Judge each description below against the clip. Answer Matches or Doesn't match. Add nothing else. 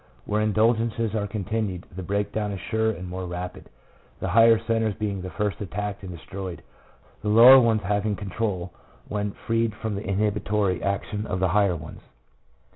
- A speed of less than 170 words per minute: Doesn't match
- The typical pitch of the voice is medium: Doesn't match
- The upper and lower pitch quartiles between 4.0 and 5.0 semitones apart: Doesn't match